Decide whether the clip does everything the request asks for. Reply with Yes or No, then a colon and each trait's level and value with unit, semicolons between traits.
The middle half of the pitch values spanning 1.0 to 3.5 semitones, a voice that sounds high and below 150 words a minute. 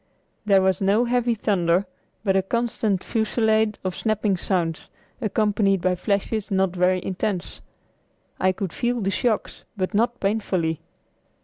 Yes: average, 2.8 semitones; high, 200 Hz; slow, 135 wpm